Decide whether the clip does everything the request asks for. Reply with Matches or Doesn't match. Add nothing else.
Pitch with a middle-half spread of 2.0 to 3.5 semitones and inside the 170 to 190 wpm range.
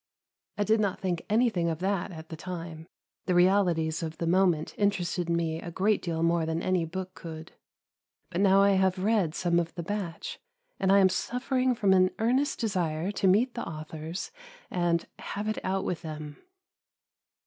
Matches